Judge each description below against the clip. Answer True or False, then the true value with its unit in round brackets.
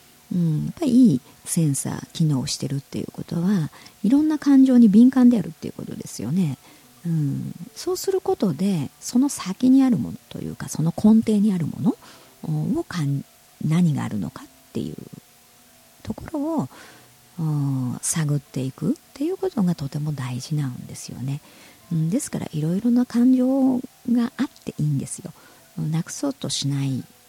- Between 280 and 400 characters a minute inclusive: True (325 characters per minute)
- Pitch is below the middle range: False (175 Hz)